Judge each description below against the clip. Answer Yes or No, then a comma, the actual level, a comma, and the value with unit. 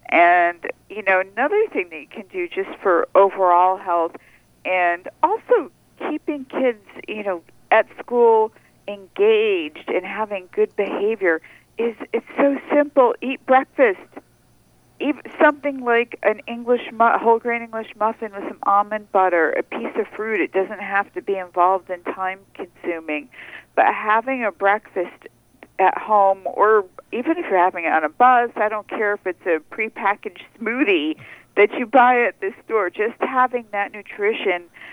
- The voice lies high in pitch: Yes, high, 220 Hz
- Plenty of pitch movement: Yes, wide, 7.1 semitones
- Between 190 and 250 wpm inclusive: No, average, 160 wpm